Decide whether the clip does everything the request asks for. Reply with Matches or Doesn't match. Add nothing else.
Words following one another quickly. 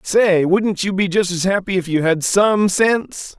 Matches